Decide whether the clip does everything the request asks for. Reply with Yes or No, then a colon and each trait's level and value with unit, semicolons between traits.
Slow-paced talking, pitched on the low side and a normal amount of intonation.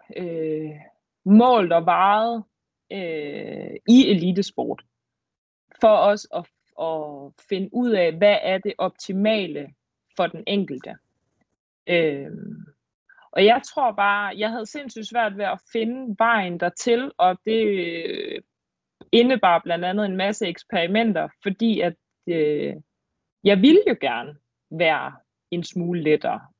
No: slow, 125 wpm; high, 200 Hz; average, 4.5 semitones